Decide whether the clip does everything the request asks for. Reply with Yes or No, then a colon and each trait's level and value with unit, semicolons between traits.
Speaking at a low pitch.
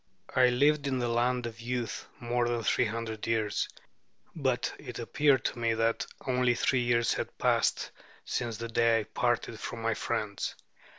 Yes: low, 120 Hz